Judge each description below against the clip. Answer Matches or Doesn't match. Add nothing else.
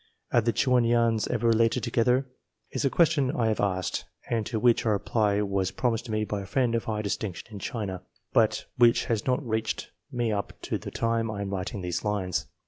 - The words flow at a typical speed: Doesn't match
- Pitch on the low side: Matches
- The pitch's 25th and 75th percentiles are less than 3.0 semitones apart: Matches